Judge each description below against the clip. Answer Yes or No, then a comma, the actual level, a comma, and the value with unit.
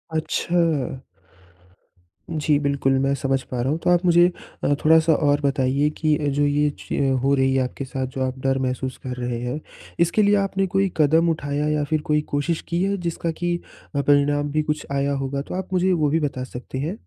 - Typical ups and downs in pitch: Yes, average, 3.1 semitones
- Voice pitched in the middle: Yes, medium, 145 Hz